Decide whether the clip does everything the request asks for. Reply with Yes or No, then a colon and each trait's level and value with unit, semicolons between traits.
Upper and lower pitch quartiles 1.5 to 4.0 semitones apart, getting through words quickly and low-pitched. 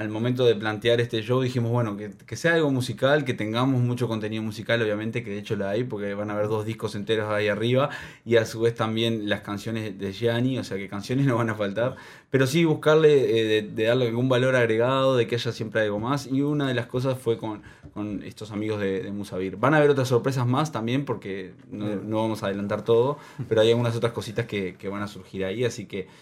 Yes: average, 3.1 semitones; fast, 245 wpm; low, 115 Hz